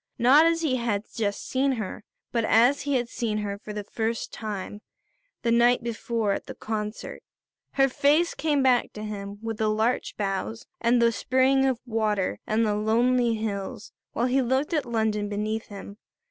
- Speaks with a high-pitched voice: Yes, high, 230 Hz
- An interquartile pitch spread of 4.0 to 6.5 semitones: No, average, 3.2 semitones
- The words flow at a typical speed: Yes, average, 180 wpm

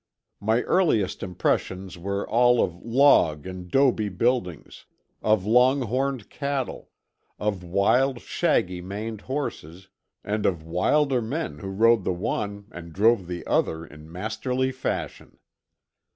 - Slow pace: Yes, slow, 125 wpm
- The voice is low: Yes, low, 105 Hz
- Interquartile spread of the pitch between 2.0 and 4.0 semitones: No, wide, 5.4 semitones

